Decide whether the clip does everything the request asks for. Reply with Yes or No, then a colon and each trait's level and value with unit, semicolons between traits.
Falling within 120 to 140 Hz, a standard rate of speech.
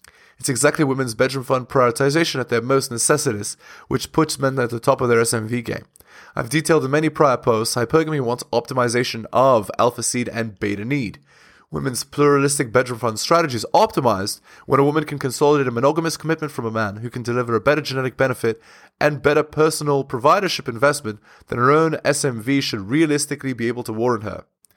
Yes: low, 135 Hz; average, 185 wpm